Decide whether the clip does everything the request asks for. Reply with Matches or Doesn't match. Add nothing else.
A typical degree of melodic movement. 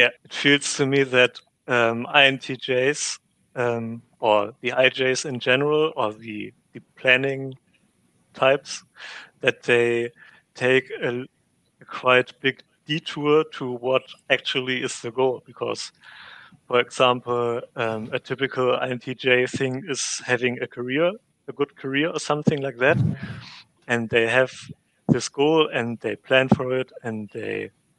Doesn't match